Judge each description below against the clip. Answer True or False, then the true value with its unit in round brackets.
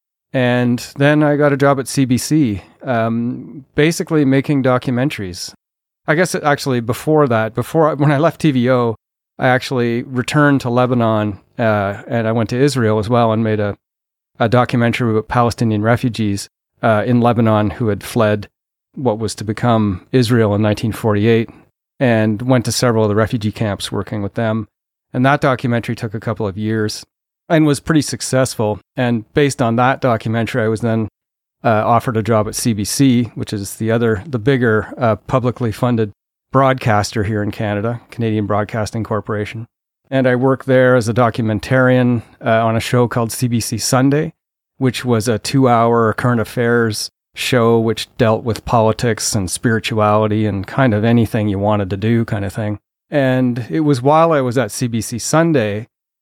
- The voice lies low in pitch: True (115 Hz)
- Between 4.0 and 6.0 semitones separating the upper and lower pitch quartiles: False (2.9 semitones)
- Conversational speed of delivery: True (170 wpm)